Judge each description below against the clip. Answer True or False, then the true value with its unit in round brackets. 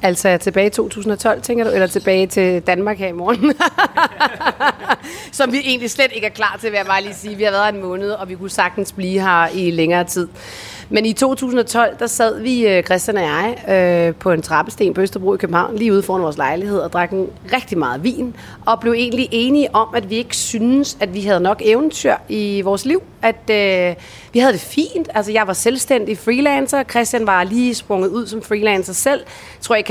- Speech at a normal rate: True (215 wpm)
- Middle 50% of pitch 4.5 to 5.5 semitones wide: False (3.9 semitones)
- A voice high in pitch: True (210 Hz)